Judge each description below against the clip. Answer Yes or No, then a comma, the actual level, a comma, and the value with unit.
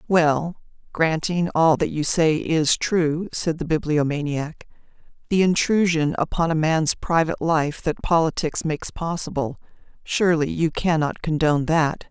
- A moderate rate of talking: No, slow, 130 wpm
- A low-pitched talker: No, medium, 160 Hz